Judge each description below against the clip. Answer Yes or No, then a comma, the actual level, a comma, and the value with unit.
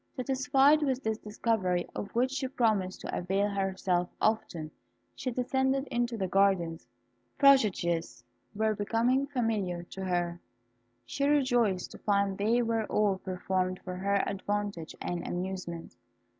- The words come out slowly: Yes, slow, 130 wpm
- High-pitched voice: Yes, high, 205 Hz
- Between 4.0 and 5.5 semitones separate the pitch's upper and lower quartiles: Yes, average, 4.8 semitones